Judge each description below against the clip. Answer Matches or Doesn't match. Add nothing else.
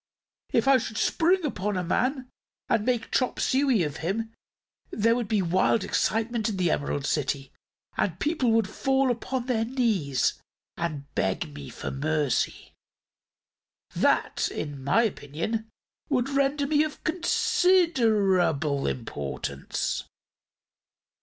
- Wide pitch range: Matches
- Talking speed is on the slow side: Matches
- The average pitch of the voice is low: Doesn't match